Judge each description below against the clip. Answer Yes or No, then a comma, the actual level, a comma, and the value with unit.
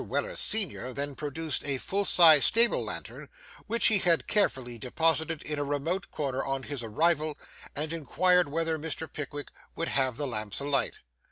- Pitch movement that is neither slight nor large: Yes, average, 3.3 semitones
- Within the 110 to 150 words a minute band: No, average, 165 wpm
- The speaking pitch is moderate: Yes, medium, 150 Hz